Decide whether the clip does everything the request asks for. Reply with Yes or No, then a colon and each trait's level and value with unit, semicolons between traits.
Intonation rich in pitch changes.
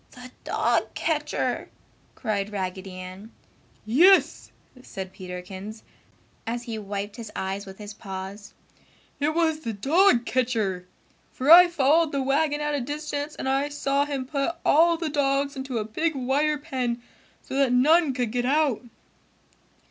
Yes: wide, 5.8 semitones